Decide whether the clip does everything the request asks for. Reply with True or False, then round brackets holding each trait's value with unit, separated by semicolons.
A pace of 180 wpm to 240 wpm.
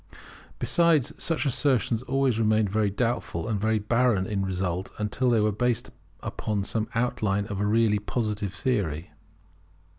False (145 wpm)